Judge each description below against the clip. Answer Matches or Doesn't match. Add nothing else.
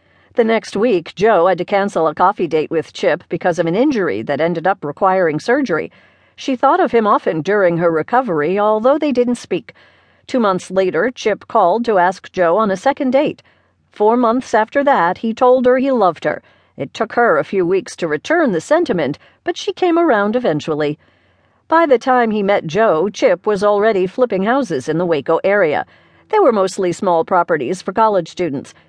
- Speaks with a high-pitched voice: Matches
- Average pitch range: Doesn't match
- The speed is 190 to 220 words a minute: Matches